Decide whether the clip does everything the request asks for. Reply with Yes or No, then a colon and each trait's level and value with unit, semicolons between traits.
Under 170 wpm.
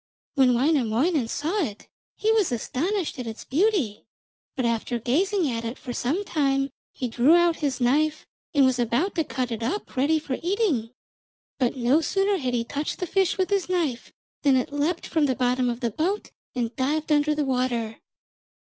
No: average, 185 wpm